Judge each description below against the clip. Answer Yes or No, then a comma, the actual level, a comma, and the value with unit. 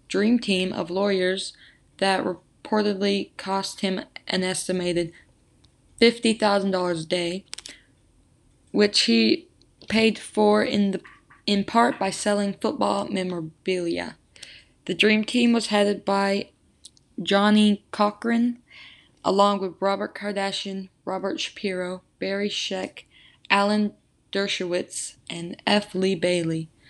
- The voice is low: No, high, 195 Hz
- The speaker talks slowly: Yes, slow, 105 wpm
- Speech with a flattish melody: Yes, narrow, 2.0 semitones